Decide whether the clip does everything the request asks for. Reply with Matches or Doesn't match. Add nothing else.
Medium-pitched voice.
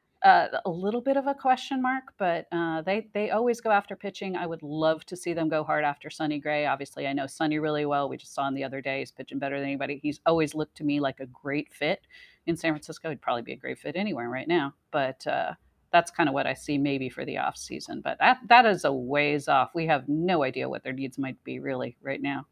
Matches